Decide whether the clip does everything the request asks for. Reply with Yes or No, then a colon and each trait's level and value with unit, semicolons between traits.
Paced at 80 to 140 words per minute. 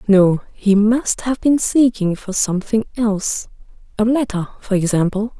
Yes: slow, 135 wpm